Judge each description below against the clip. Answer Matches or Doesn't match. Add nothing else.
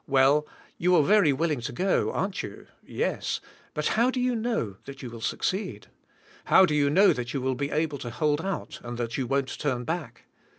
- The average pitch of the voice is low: Doesn't match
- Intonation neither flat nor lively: Doesn't match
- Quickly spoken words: Matches